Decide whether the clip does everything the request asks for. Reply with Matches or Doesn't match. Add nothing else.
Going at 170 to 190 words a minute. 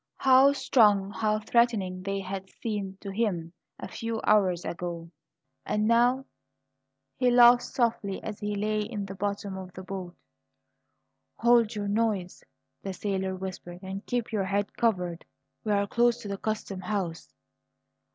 Doesn't match